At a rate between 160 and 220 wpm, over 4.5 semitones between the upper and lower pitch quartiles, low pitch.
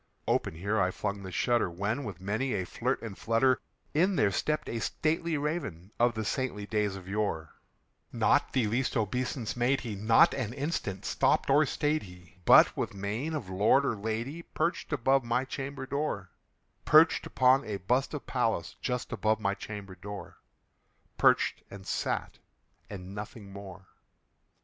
Yes: average, 165 wpm; average, 5.2 semitones; low, 110 Hz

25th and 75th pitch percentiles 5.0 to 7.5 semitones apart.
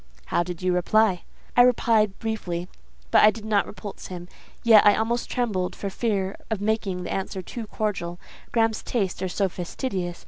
No: average, 3.4 semitones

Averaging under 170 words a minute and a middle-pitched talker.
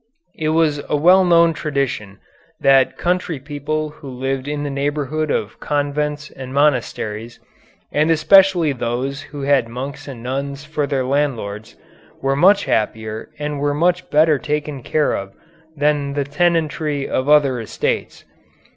Yes: average, 145 wpm; medium, 145 Hz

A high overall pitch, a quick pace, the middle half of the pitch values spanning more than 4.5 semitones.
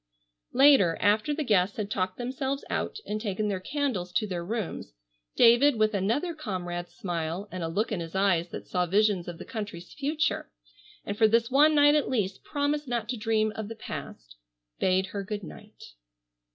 No: high, 210 Hz; average, 185 wpm; wide, 5.4 semitones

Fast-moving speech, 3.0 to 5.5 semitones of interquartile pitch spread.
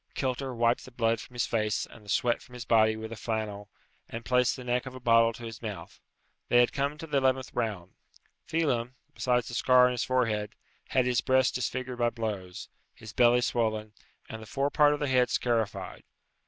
No: fast, 210 wpm; narrow, 2.5 semitones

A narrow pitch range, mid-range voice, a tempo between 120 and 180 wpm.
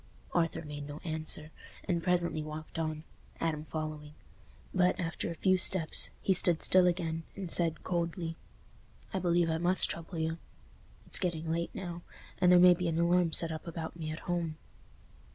Yes: narrow, 1.9 semitones; medium, 165 Hz; average, 170 wpm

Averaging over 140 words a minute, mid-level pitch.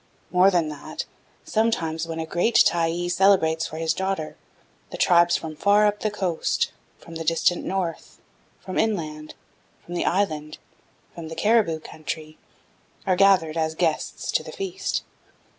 Yes: average, 150 wpm; medium, 170 Hz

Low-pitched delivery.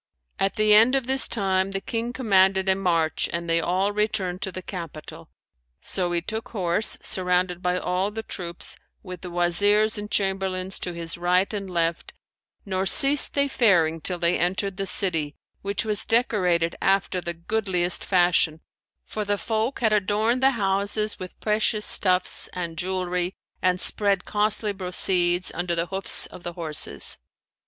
No: high, 190 Hz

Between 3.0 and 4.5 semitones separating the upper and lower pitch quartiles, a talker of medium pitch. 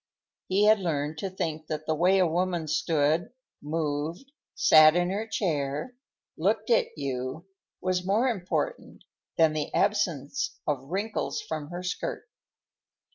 Yes: average, 4.0 semitones; medium, 170 Hz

